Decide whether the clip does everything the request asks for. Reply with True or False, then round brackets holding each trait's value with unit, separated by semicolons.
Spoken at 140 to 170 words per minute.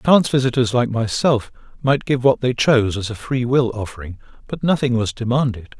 False (185 wpm)